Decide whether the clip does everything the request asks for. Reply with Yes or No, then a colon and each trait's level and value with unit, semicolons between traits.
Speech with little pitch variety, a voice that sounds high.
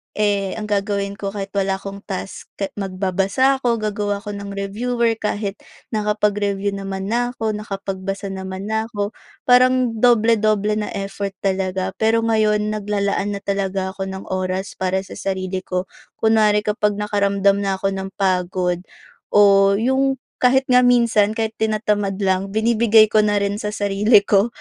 Yes: narrow, 1.9 semitones; high, 205 Hz